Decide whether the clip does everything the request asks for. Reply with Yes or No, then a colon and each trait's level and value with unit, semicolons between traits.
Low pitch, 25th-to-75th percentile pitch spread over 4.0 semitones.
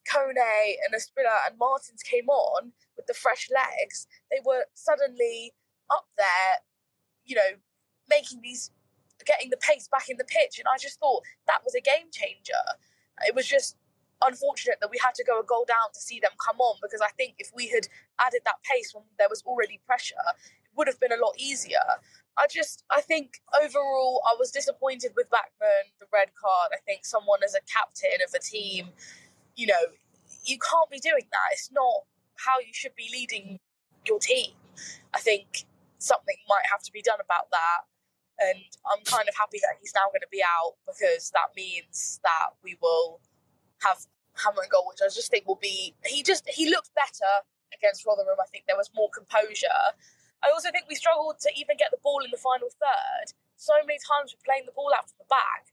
No: very high, 280 Hz; average, 5.1 semitones